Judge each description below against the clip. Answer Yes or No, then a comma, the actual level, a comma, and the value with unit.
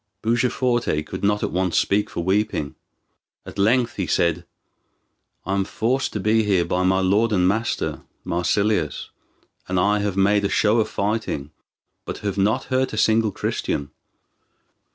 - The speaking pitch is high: No, low, 100 Hz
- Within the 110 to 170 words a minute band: Yes, average, 155 wpm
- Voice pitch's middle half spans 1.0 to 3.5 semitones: Yes, average, 3.0 semitones